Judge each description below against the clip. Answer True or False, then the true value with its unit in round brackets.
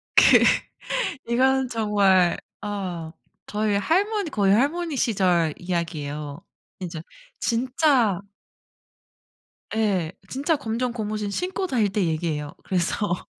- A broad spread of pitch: True (6.4 semitones)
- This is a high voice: True (205 Hz)